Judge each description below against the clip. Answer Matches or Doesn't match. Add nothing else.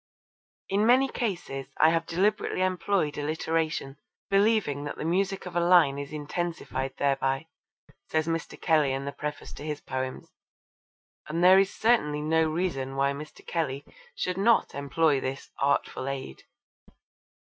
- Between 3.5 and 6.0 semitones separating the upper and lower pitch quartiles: Matches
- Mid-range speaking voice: Matches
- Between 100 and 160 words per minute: Matches